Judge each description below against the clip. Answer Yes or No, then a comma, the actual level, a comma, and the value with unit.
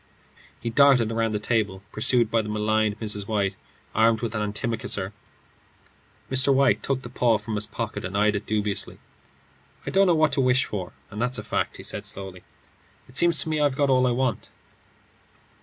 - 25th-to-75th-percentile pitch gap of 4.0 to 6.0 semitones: No, average, 3.6 semitones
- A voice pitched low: Yes, low, 115 Hz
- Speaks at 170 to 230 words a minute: Yes, average, 190 wpm